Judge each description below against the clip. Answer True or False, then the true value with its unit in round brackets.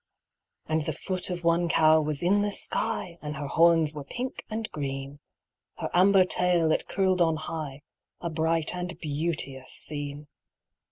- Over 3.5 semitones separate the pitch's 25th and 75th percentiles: False (3.1 semitones)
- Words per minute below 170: True (160 wpm)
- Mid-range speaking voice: True (160 Hz)